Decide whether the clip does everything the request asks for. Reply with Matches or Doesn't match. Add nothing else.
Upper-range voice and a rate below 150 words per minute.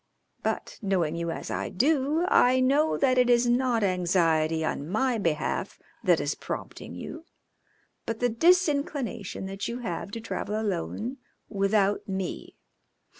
Matches